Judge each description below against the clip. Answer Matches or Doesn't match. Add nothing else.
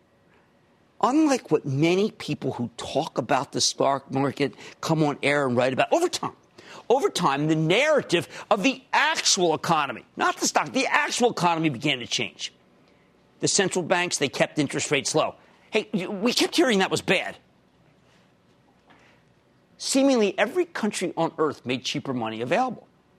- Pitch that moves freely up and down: Matches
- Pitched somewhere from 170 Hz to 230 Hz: Doesn't match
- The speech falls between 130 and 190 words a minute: Matches